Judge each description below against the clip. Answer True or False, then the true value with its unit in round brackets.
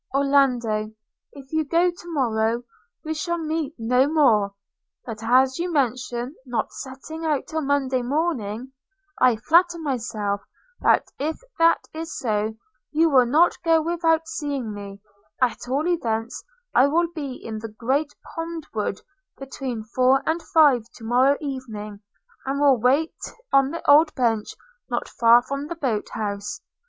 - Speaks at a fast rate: False (150 wpm)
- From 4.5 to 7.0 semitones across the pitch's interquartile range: True (5.4 semitones)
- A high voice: True (265 Hz)